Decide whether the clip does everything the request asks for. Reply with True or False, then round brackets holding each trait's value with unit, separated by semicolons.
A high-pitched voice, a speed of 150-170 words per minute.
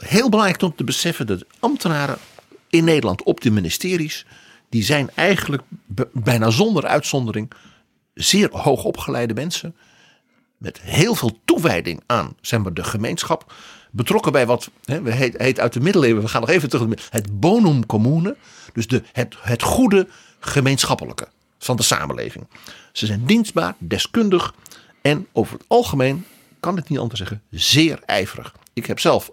False (140 Hz; 155 wpm)